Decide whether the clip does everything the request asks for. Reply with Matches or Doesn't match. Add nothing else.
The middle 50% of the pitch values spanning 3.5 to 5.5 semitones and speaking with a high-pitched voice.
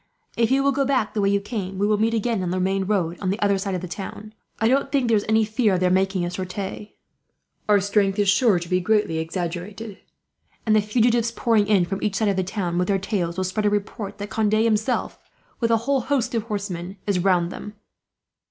Doesn't match